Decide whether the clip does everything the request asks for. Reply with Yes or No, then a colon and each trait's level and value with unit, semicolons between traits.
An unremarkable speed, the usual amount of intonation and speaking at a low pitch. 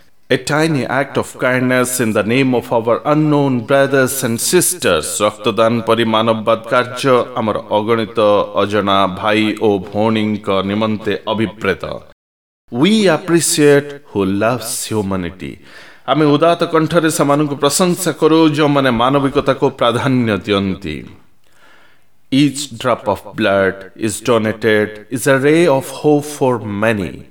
No: slow, 90 wpm; average, 5.0 semitones; low, 120 Hz